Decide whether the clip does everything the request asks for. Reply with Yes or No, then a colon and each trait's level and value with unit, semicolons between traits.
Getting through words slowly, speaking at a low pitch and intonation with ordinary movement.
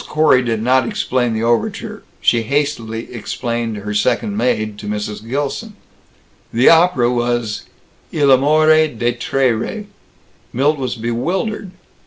Yes: slow, 130 wpm; low, 120 Hz; average, 4.3 semitones